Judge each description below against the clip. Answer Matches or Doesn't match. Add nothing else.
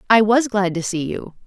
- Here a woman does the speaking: Matches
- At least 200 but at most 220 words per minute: Doesn't match